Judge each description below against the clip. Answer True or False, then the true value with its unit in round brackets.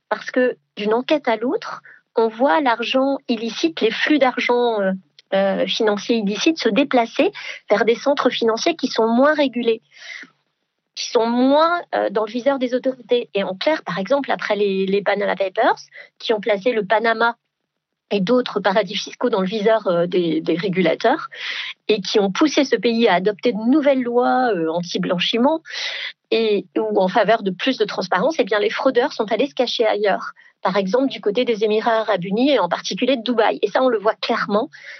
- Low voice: False (230 Hz)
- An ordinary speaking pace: True (185 wpm)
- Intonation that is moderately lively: True (3.8 semitones)